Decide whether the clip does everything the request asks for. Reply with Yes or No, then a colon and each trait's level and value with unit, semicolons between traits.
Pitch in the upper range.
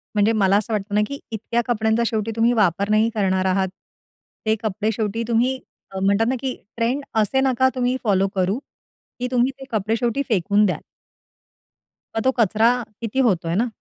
Yes: high, 220 Hz